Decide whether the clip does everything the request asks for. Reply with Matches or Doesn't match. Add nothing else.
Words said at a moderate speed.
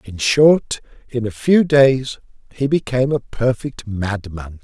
Matches